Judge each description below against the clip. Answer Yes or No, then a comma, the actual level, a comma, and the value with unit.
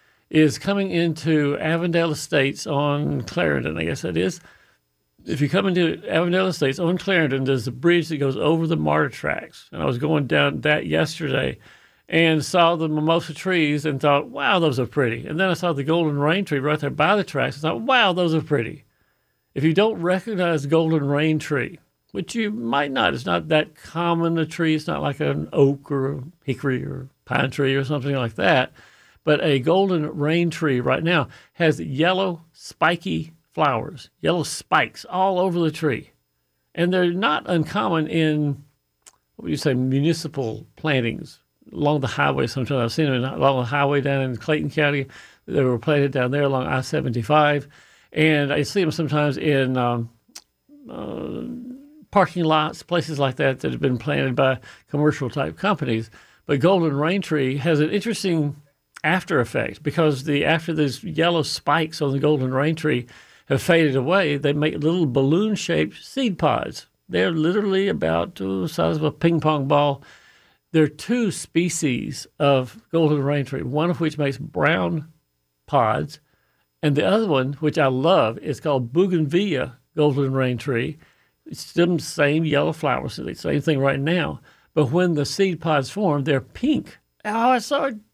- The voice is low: No, medium, 150 Hz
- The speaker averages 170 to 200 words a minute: Yes, average, 175 wpm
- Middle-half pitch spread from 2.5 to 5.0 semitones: Yes, average, 3.5 semitones